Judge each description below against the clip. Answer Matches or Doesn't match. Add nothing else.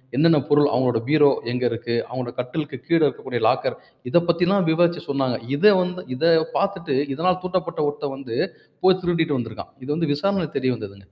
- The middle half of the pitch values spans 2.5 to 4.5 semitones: Doesn't match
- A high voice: Doesn't match